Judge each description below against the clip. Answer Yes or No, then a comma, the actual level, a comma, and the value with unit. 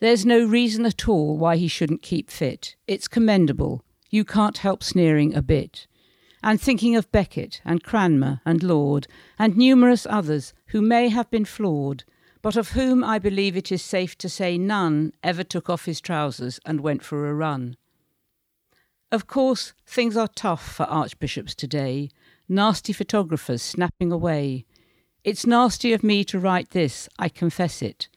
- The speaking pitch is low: No, medium, 180 Hz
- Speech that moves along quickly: No, average, 165 wpm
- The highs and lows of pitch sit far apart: Yes, wide, 5.9 semitones